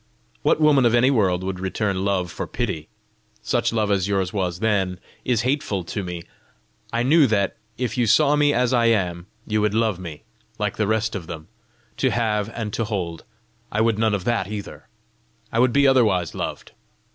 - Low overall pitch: Yes, low, 105 Hz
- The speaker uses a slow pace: No, average, 190 wpm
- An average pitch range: Yes, average, 4.1 semitones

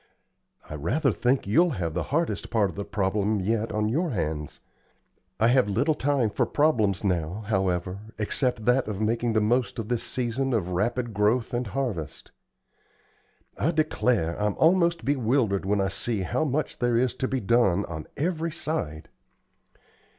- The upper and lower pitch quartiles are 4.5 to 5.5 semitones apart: Yes, average, 5.1 semitones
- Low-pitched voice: Yes, low, 115 Hz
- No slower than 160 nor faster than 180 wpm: Yes, average, 165 wpm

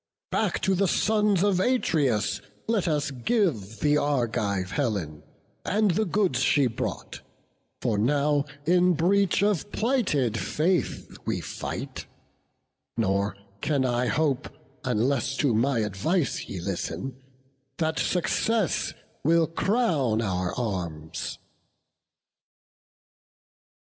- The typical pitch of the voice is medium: Yes, medium, 145 Hz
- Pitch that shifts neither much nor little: No, wide, 8.4 semitones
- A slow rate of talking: Yes, slow, 105 wpm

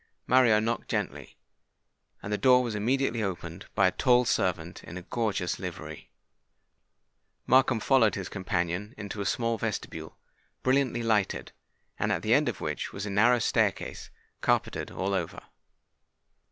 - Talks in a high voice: No, low, 105 Hz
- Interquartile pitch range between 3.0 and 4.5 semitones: Yes, average, 4.0 semitones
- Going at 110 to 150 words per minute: Yes, average, 145 wpm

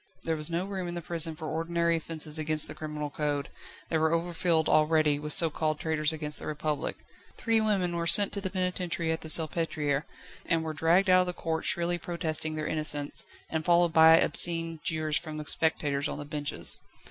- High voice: No, medium, 160 Hz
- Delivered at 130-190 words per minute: No, average, 200 wpm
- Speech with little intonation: Yes, narrow, 1.9 semitones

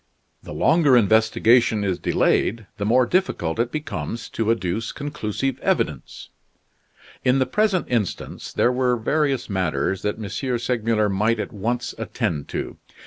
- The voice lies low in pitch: Yes, low, 115 Hz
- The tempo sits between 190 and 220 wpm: No, average, 140 wpm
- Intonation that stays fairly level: No, average, 3.6 semitones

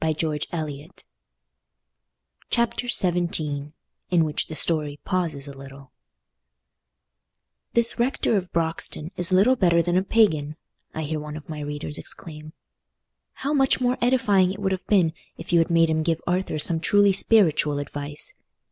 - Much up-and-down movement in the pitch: No, average, 4.1 semitones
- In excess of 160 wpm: No, average, 150 wpm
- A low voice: No, medium, 165 Hz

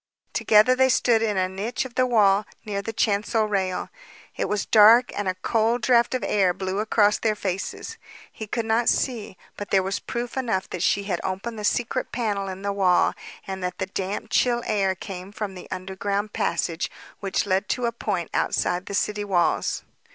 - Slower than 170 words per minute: No, average, 195 wpm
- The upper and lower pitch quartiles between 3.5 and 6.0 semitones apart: No, average, 2.9 semitones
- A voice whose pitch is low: No, high, 205 Hz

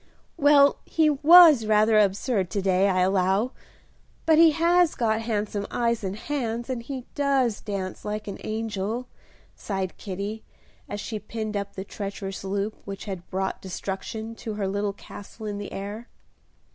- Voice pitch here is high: Yes, high, 215 Hz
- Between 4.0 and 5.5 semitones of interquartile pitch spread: No, average, 3.3 semitones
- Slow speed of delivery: No, average, 160 wpm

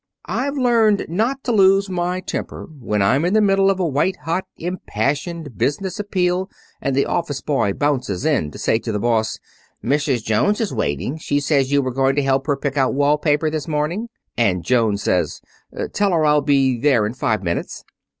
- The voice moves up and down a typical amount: No, wide, 6.4 semitones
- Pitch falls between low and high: Yes, medium, 145 Hz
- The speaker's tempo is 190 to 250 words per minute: Yes, average, 195 wpm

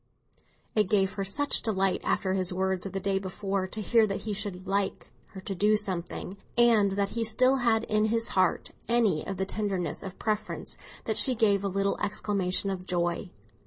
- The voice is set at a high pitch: Yes, high, 200 Hz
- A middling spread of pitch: No, narrow, 2.2 semitones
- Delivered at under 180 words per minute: No, average, 195 wpm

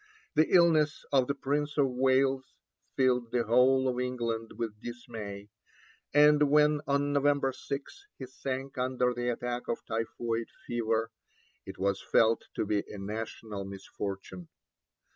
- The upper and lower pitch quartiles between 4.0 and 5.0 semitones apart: No, average, 3.6 semitones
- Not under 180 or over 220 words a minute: No, average, 140 wpm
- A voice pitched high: No, low, 125 Hz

